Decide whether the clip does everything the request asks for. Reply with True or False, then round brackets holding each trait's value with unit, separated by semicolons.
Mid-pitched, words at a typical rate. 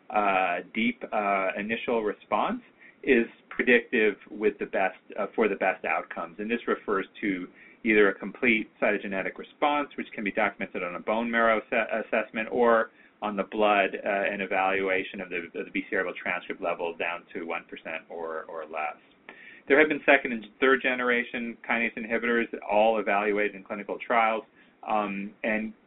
False (110 Hz; 165 wpm)